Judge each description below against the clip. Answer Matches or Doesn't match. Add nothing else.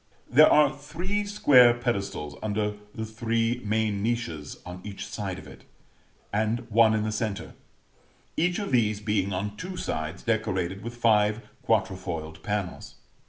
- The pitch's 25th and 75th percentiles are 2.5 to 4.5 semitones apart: Matches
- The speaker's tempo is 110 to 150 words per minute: Matches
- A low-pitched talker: Matches